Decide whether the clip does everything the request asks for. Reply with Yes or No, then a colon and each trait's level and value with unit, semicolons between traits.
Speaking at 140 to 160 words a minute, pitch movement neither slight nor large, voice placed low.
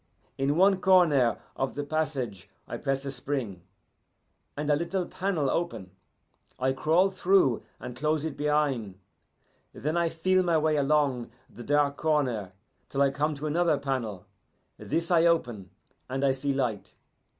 No: average, 150 wpm; average, 3.6 semitones; medium, 145 Hz